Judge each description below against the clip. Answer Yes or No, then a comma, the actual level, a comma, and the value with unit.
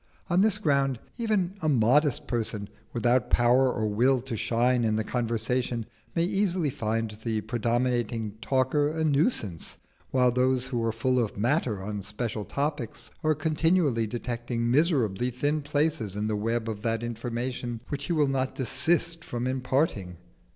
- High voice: No, low, 125 Hz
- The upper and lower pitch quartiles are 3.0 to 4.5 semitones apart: Yes, average, 4.2 semitones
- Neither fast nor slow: Yes, average, 155 wpm